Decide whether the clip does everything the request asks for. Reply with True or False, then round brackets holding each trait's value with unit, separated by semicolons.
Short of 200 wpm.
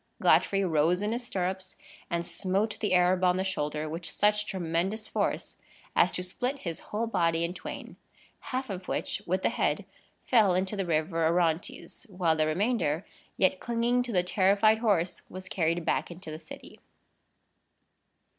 True (165 wpm)